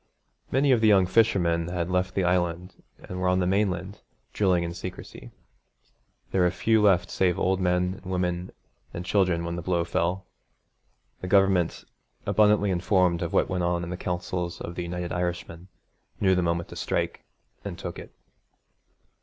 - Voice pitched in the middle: No, very low, 90 Hz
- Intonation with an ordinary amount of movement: No, narrow, 1.6 semitones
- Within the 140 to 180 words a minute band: Yes, average, 170 wpm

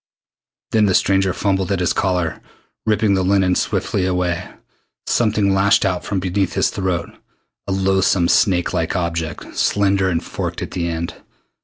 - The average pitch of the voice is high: No, very low, 95 Hz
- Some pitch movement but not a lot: No, narrow, 1.9 semitones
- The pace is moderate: Yes, average, 155 wpm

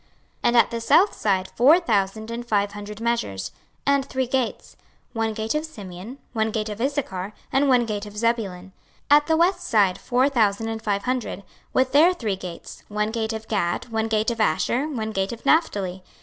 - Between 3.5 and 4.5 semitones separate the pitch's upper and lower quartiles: Yes, average, 4.0 semitones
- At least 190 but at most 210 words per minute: Yes, average, 195 wpm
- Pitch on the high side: Yes, high, 225 Hz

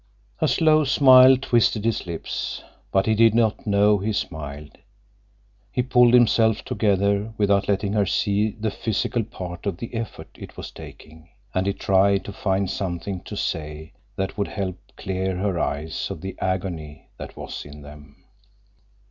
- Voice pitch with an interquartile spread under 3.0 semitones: No, average, 3.6 semitones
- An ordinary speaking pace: Yes, average, 160 wpm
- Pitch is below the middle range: Yes, low, 100 Hz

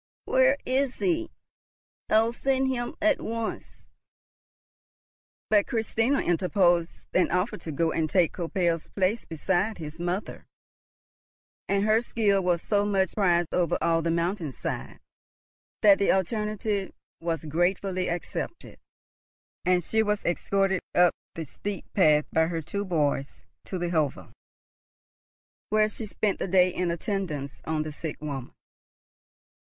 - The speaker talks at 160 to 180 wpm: No, slow, 135 wpm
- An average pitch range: Yes, average, 4.1 semitones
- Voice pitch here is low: No, medium, 185 Hz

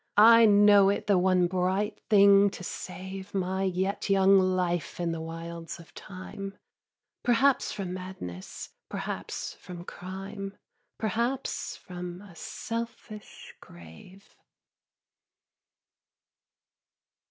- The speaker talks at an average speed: No, slow, 100 wpm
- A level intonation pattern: Yes, narrow, 2.2 semitones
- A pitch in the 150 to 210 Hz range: Yes, high, 190 Hz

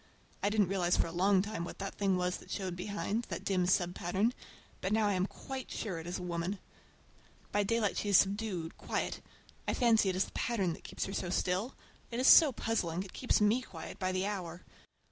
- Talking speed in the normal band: No, fast, 215 wpm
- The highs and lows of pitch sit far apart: No, average, 2.9 semitones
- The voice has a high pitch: Yes, high, 195 Hz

